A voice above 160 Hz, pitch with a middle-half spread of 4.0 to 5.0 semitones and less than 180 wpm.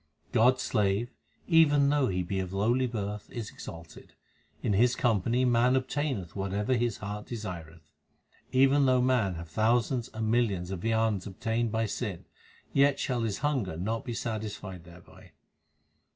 No: low, 110 Hz; average, 4.4 semitones; average, 150 wpm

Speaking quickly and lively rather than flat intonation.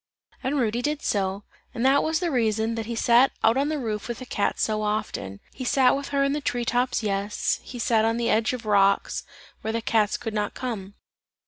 No: fast, 230 wpm; average, 3.3 semitones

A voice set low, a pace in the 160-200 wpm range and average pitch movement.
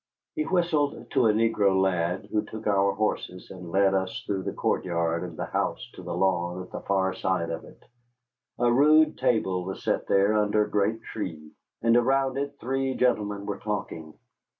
Yes: low, 100 Hz; average, 190 wpm; average, 4.2 semitones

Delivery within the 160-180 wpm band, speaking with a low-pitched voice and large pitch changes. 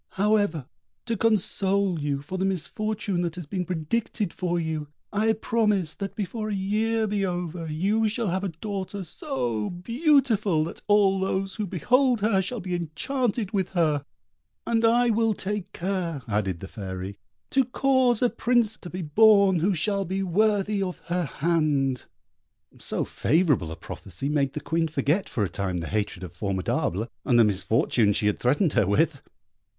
No: average, 170 wpm; medium, 185 Hz; wide, 6.0 semitones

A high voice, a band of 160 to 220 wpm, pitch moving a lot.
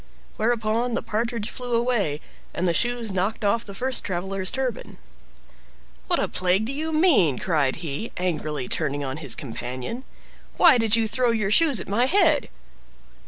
Yes: high, 215 Hz; average, 165 wpm; wide, 5.9 semitones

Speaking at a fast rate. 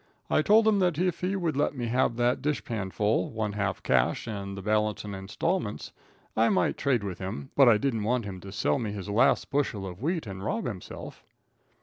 Yes: fast, 215 wpm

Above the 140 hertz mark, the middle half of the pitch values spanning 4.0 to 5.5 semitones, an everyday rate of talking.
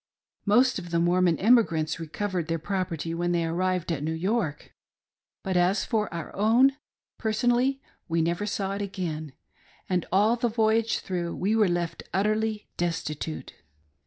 Yes: medium, 185 Hz; average, 4.3 semitones; average, 155 wpm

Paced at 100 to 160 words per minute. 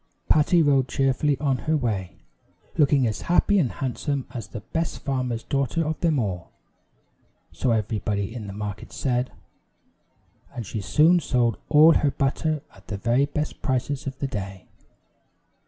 Yes: average, 155 wpm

